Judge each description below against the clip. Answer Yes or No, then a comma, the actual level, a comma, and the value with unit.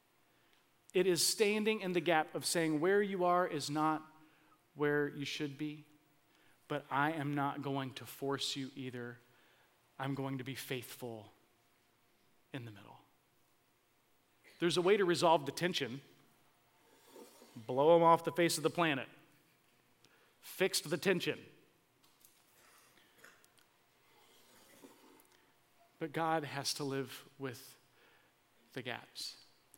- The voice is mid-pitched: Yes, medium, 145 Hz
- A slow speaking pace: Yes, slow, 120 wpm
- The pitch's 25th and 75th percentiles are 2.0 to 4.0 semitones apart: Yes, average, 3.7 semitones